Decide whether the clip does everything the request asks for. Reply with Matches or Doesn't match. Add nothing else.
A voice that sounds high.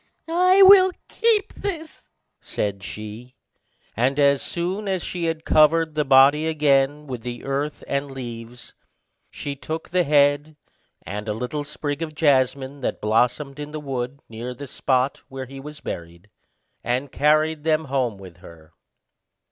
Doesn't match